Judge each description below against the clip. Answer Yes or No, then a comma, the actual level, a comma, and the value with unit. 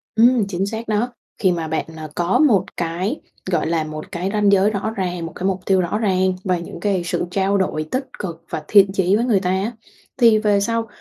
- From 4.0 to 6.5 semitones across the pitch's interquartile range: No, average, 3.3 semitones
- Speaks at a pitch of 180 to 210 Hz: Yes, high, 190 Hz